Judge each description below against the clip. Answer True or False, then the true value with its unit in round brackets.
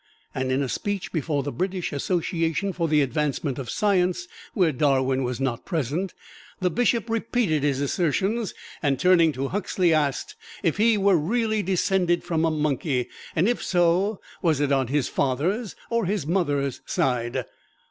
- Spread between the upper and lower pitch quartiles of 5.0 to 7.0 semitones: True (5.5 semitones)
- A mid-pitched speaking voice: True (165 Hz)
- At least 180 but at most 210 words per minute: False (160 wpm)